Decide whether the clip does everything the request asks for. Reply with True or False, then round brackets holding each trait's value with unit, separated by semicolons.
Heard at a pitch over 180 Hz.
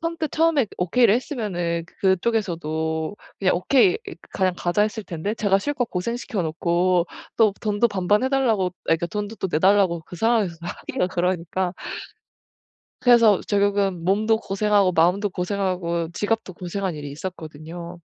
True (190 Hz)